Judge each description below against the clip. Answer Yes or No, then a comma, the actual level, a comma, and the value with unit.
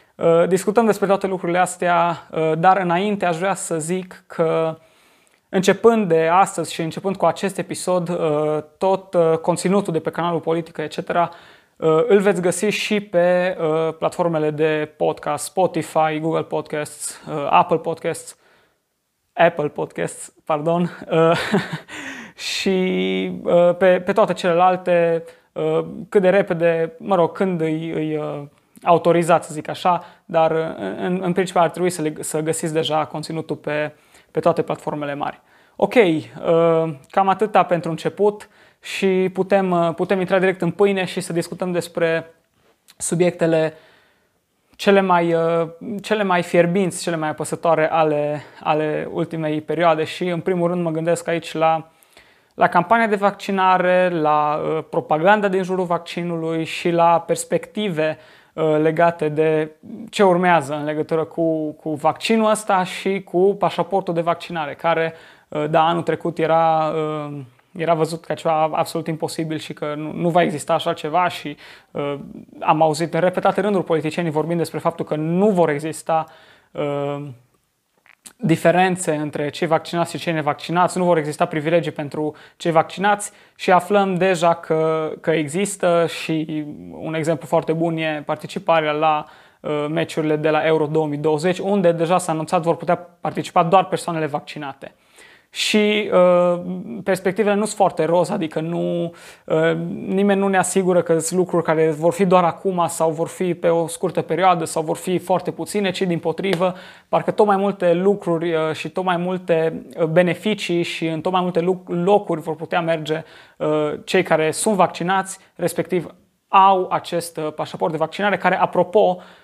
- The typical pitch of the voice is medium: Yes, medium, 170 Hz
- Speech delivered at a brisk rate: No, average, 145 wpm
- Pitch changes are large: No, narrow, 2.5 semitones